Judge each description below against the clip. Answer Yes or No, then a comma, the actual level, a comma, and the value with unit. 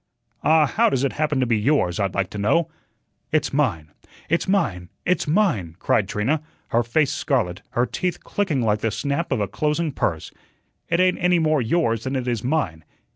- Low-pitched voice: Yes, low, 130 Hz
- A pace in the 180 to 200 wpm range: Yes, average, 190 wpm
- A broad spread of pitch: Yes, wide, 7.0 semitones